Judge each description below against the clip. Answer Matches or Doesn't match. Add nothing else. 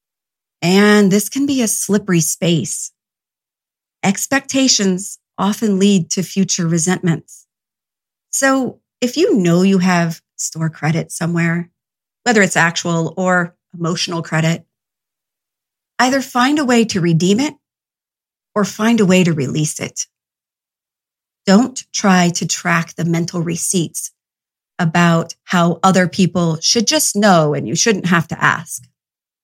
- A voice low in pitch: Doesn't match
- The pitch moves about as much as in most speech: Matches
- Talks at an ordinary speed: Doesn't match